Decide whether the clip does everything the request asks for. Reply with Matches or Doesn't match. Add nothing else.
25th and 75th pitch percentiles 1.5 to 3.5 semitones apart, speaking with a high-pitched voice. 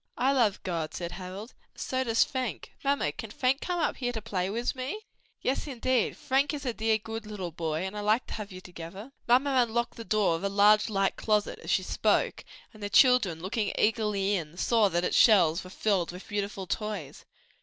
Doesn't match